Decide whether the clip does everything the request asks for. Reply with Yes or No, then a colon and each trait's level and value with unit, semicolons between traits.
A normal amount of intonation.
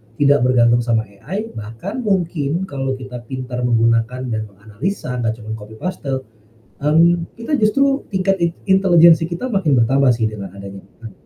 No: wide, 7.6 semitones